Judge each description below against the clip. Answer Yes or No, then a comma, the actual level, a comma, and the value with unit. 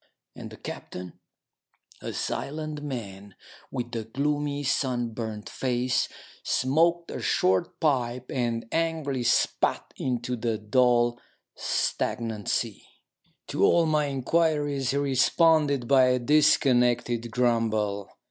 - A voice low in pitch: Yes, low, 125 Hz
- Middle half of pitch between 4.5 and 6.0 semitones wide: No, average, 3.7 semitones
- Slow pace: Yes, slow, 110 wpm